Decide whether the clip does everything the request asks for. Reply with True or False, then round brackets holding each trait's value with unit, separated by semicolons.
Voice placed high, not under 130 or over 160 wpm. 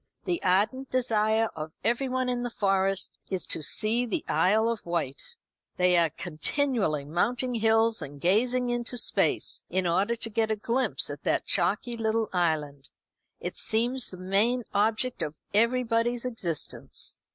True (220 Hz; 150 wpm)